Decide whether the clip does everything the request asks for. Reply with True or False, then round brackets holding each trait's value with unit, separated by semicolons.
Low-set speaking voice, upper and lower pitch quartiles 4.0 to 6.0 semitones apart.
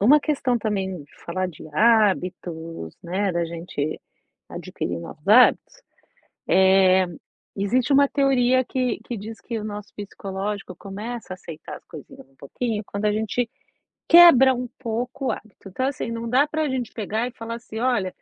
False (215 Hz; 4.7 semitones)